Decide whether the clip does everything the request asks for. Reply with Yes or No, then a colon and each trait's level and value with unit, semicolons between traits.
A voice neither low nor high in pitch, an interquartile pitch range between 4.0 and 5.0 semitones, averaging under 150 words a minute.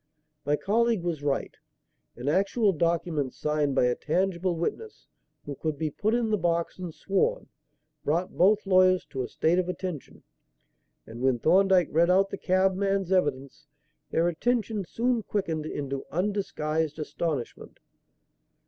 Yes: medium, 175 Hz; average, 4.4 semitones; average, 140 wpm